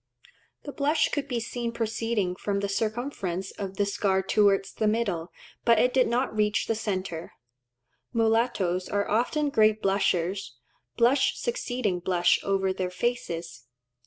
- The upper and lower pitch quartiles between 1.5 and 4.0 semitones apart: Yes, average, 3.7 semitones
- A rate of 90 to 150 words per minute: Yes, average, 140 wpm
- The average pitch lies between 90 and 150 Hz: No, high, 210 Hz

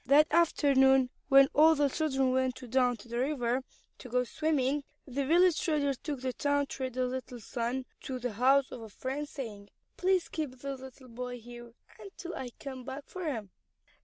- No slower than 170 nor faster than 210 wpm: Yes, average, 180 wpm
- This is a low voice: No, very high, 265 Hz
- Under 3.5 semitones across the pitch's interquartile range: Yes, narrow, 2.5 semitones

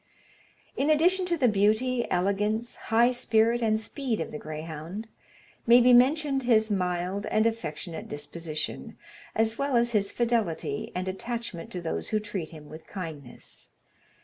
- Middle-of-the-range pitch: No, high, 215 Hz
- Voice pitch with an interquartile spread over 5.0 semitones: Yes, wide, 5.4 semitones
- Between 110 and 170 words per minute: Yes, average, 150 wpm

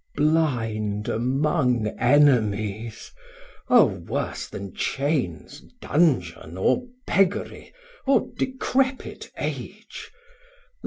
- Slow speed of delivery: Yes, slow, 70 wpm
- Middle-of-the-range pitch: No, low, 125 Hz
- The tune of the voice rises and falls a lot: Yes, wide, 7.2 semitones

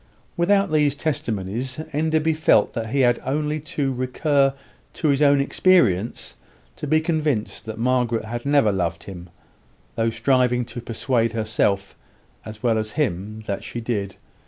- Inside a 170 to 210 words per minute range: No, average, 150 wpm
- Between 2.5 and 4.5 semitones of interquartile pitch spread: No, average, 5.1 semitones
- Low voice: Yes, low, 125 Hz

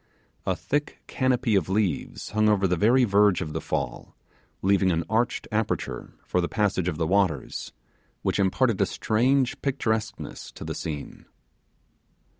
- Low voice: Yes, low, 105 Hz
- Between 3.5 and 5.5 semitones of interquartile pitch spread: Yes, average, 4.3 semitones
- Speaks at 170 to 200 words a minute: No, average, 150 wpm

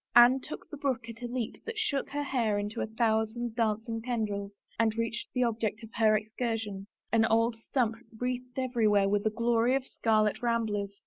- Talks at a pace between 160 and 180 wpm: No, average, 190 wpm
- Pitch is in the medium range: No, high, 230 Hz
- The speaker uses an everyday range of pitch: No, narrow, 2.1 semitones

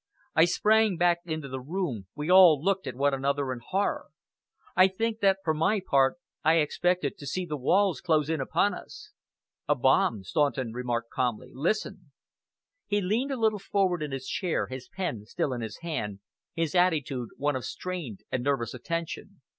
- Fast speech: No, average, 180 wpm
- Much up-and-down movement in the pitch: Yes, wide, 5.9 semitones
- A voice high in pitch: No, medium, 155 Hz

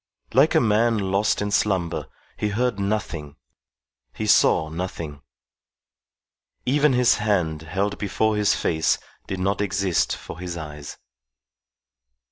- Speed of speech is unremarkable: No, slow, 120 wpm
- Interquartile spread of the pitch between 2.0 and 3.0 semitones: No, average, 4.1 semitones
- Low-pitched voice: Yes, low, 100 Hz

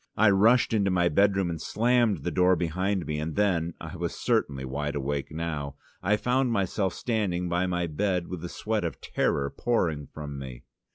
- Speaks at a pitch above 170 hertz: No, very low, 90 Hz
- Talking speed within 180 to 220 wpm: Yes, average, 185 wpm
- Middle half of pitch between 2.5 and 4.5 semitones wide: No, average, 5.0 semitones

